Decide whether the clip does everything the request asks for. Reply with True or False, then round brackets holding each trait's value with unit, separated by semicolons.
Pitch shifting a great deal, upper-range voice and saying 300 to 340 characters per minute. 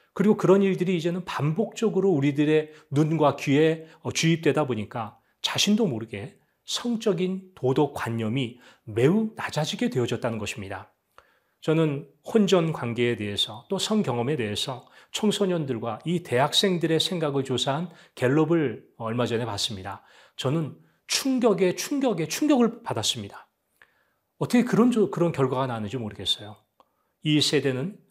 False (7.4 semitones; 150 Hz; 305 characters per minute)